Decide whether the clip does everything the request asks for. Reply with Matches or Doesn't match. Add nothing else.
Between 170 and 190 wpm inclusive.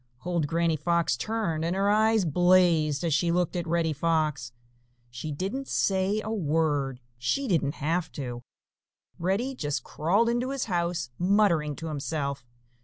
Doesn't match